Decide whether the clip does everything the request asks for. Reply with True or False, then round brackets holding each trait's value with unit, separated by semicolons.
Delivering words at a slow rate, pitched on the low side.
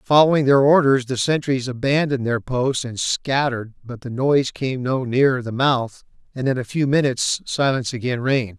False (180 wpm; 130 Hz)